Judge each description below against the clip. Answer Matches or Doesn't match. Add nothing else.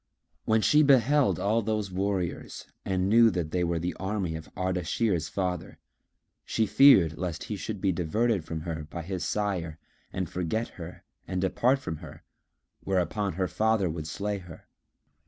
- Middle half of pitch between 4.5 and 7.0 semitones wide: Doesn't match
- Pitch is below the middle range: Matches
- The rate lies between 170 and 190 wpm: Doesn't match